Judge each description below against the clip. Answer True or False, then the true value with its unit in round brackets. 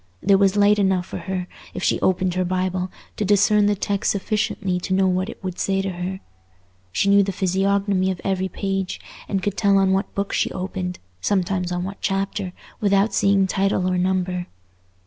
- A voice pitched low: False (190 Hz)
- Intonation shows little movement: True (1.3 semitones)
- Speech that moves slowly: False (190 wpm)